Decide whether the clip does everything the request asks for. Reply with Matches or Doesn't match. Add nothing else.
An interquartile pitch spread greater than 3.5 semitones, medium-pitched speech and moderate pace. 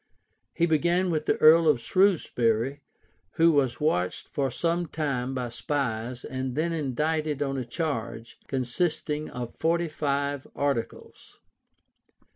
Doesn't match